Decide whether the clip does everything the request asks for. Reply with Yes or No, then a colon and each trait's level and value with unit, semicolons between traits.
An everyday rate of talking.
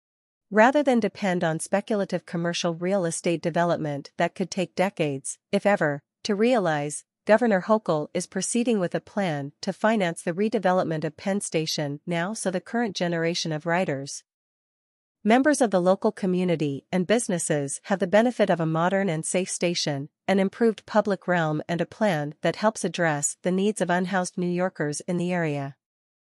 Yes: average, 165 wpm